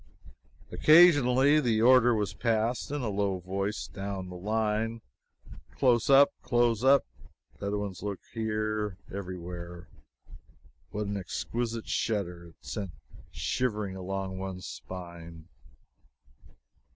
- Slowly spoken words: Yes, slow, 110 wpm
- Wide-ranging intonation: No, average, 3.9 semitones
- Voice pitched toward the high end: No, low, 105 Hz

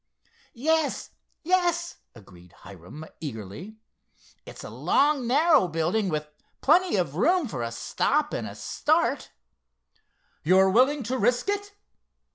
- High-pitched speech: Yes, high, 220 Hz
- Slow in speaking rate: Yes, slow, 120 wpm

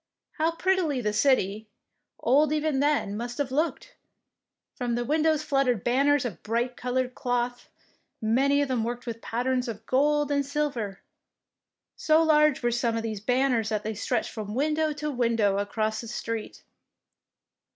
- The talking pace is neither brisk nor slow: Yes, average, 160 wpm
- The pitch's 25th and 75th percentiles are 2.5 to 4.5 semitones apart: Yes, average, 4.2 semitones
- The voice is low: No, very high, 250 Hz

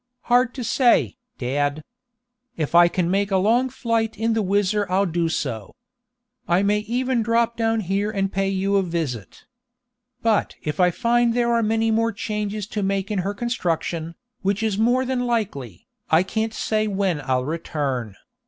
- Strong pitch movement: No, average, 4.7 semitones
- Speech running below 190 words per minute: Yes, average, 170 wpm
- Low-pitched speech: No, high, 200 Hz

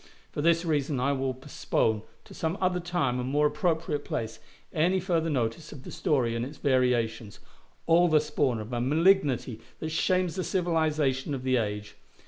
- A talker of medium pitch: Yes, medium, 145 Hz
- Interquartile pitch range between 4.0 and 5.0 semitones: Yes, average, 4.6 semitones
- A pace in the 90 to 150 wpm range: No, average, 175 wpm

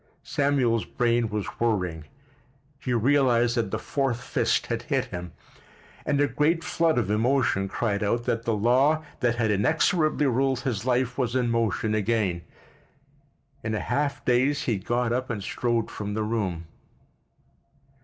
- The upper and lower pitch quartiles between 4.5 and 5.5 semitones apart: No, average, 3.8 semitones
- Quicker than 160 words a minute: No, average, 155 wpm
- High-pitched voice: No, low, 120 Hz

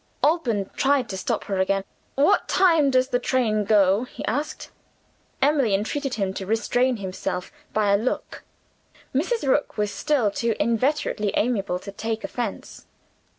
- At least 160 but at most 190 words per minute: No, average, 150 wpm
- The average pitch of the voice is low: No, high, 230 Hz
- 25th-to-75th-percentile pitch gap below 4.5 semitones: No, average, 5.2 semitones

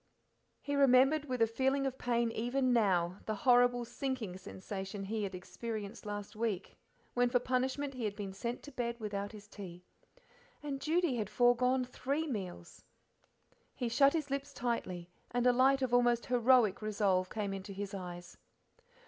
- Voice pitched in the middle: No, high, 235 Hz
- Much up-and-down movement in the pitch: No, average, 4.2 semitones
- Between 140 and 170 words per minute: Yes, average, 165 wpm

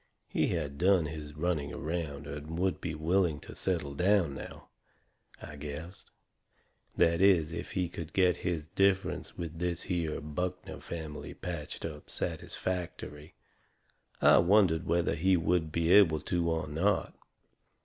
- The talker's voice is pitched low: Yes, very low, 85 Hz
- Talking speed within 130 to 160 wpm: Yes, average, 140 wpm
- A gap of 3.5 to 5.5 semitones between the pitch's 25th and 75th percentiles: No, average, 2.7 semitones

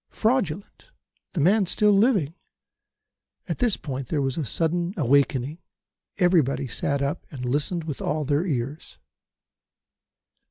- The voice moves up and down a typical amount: Yes, average, 4.8 semitones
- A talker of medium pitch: Yes, medium, 155 Hz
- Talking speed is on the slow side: Yes, slow, 125 wpm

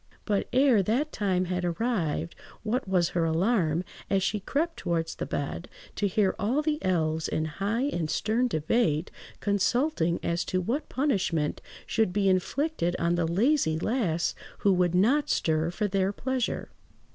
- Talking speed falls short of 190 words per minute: Yes, average, 160 wpm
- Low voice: No, high, 190 Hz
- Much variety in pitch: Yes, wide, 5.8 semitones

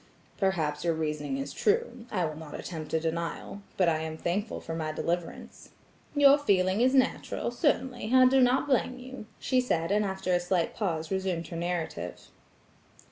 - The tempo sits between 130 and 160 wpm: No, average, 175 wpm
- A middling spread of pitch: No, wide, 7.2 semitones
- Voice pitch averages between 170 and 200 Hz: Yes, medium, 185 Hz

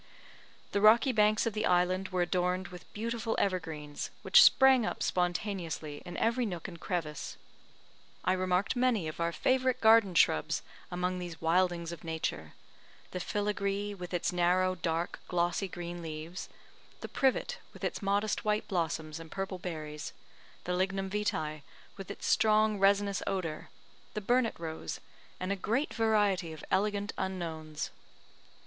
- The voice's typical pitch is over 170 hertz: Yes, medium, 185 Hz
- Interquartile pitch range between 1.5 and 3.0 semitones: No, average, 3.5 semitones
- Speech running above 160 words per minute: No, average, 145 wpm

